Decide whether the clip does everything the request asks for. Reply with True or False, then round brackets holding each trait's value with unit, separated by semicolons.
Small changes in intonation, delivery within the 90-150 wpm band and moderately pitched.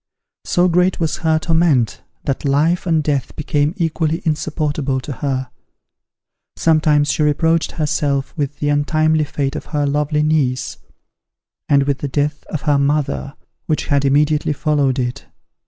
True (1.9 semitones; 145 wpm; 150 Hz)